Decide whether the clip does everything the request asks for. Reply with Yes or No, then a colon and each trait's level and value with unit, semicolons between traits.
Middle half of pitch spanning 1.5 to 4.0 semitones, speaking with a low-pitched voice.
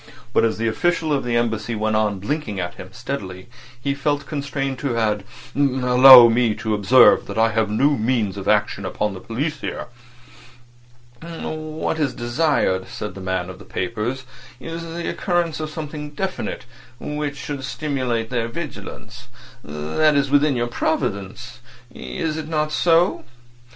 No: wide, 5.6 semitones; low, 125 Hz